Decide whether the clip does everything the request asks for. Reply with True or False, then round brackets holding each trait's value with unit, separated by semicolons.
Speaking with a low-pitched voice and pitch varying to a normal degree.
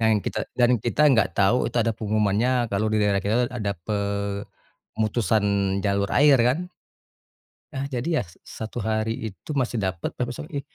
True (110 Hz; 3.3 semitones)